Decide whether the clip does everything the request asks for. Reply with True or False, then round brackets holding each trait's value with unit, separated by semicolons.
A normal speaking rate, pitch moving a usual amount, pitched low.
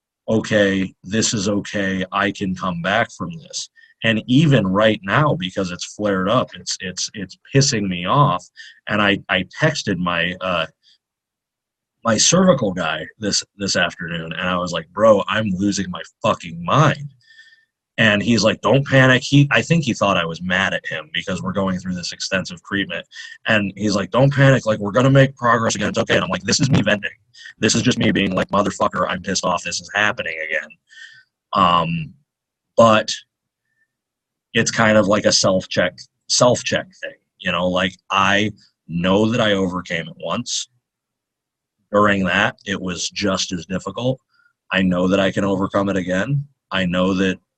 False (175 wpm; 6.2 semitones; 105 Hz)